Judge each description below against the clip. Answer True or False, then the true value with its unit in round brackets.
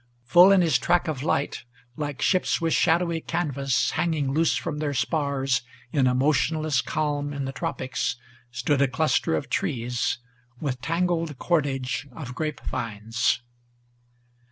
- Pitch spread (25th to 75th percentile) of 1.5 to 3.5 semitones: False (3.9 semitones)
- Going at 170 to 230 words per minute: False (140 wpm)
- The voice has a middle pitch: True (145 Hz)